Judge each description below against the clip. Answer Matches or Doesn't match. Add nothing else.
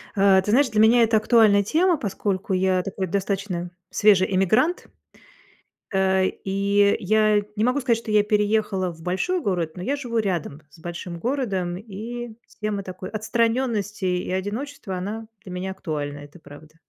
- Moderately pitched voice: Doesn't match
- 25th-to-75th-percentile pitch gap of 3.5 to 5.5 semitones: Doesn't match